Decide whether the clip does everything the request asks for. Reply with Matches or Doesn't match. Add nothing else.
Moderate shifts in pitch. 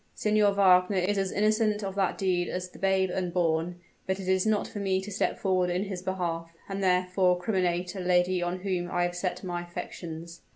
Doesn't match